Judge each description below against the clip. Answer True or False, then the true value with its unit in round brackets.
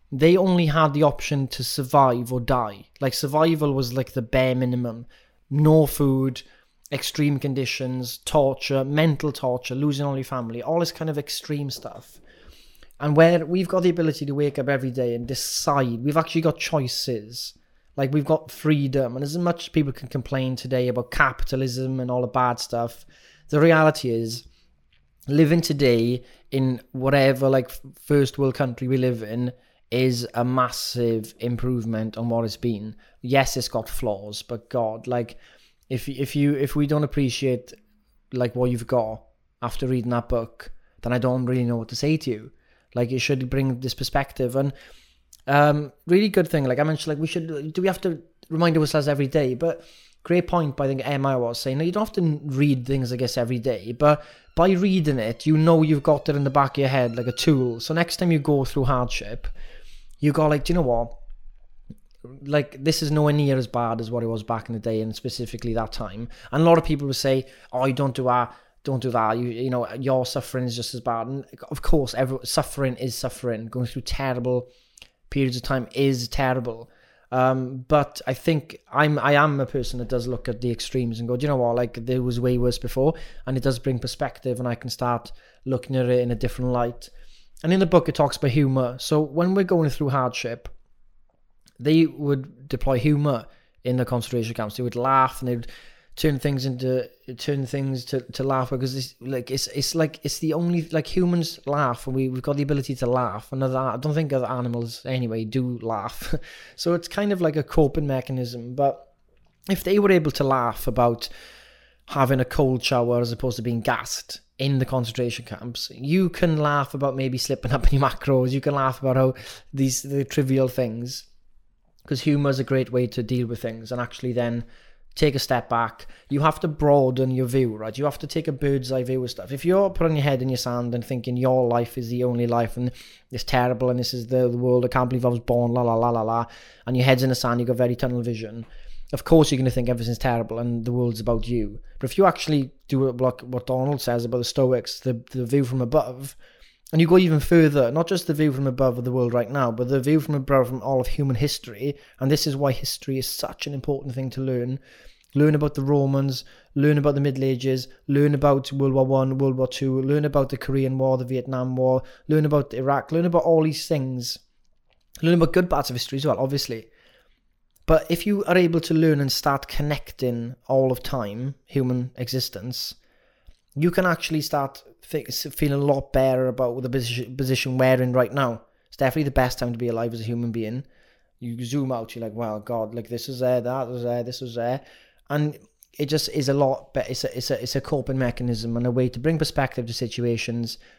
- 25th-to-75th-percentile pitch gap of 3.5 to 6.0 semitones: False (2.9 semitones)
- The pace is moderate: False (215 wpm)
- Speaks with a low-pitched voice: True (130 Hz)